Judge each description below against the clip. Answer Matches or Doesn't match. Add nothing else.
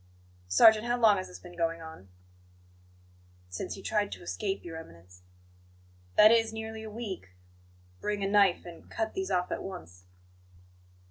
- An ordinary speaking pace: Matches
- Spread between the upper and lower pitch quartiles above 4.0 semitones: Matches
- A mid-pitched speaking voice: Doesn't match